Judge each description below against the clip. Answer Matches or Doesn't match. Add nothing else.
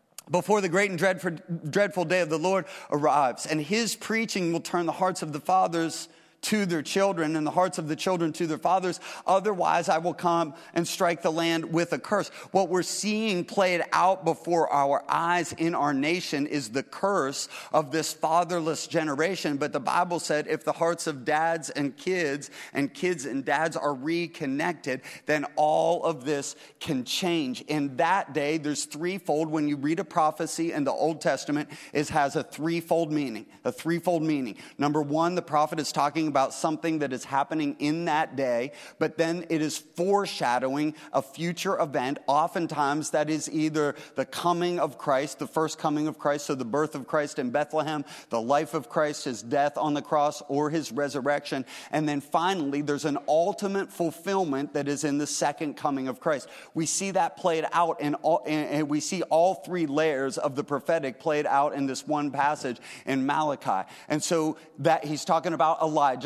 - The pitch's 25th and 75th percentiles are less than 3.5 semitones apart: Matches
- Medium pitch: Matches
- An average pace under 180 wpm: Doesn't match